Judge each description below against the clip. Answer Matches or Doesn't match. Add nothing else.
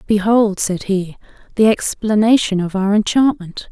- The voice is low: Doesn't match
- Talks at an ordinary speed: Doesn't match